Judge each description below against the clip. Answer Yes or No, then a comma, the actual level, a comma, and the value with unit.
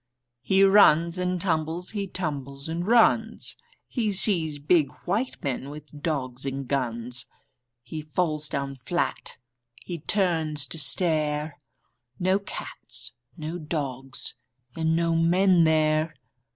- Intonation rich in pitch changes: No, average, 4.2 semitones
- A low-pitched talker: No, medium, 160 Hz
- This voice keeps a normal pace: No, slow, 125 wpm